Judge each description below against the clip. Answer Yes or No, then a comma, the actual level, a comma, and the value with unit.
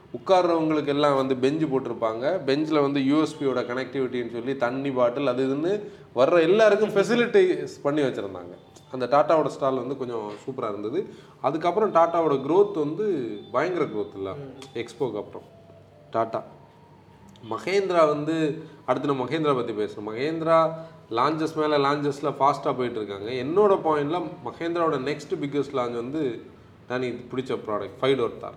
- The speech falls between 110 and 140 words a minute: Yes, average, 125 wpm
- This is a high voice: No, medium, 145 Hz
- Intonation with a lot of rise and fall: No, average, 4.3 semitones